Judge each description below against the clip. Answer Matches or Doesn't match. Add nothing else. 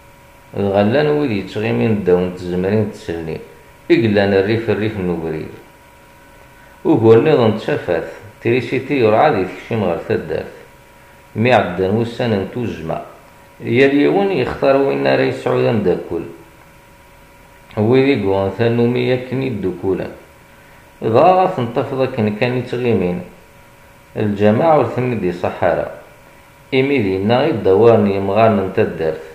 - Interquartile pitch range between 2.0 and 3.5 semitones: Doesn't match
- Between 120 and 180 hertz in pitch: Doesn't match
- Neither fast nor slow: Doesn't match